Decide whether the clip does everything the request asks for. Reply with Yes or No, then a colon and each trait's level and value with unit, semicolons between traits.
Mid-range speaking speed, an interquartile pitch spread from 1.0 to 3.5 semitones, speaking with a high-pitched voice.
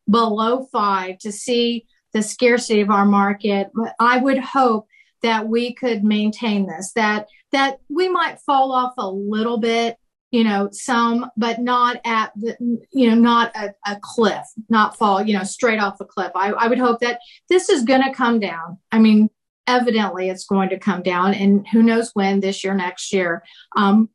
Yes: average, 185 wpm; average, 3.2 semitones; high, 225 Hz